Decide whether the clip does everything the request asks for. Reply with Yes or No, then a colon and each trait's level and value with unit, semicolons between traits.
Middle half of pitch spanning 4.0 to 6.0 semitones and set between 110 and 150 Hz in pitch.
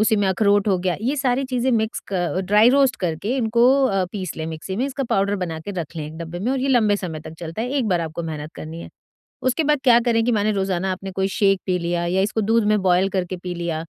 No: average, 4.9 semitones; high, 195 Hz